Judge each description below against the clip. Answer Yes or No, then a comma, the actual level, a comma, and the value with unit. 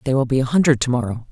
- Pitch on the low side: Yes, low, 130 Hz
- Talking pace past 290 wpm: Yes, fast, 320 wpm